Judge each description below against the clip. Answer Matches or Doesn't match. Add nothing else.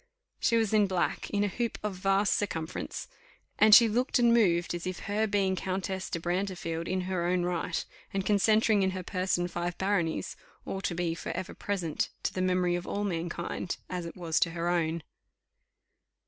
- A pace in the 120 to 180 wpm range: Doesn't match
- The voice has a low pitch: Doesn't match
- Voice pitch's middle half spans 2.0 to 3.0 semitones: Matches